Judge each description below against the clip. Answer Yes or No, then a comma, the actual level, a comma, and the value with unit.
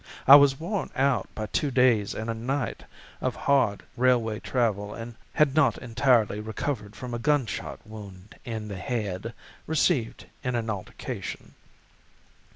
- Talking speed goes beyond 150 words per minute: No, average, 145 wpm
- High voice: No, low, 115 Hz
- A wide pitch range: No, average, 3.9 semitones